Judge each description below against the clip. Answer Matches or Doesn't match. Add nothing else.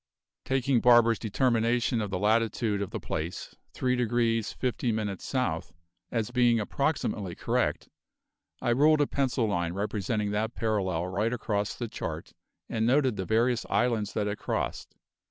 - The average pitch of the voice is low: Matches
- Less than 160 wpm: Matches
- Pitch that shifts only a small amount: Doesn't match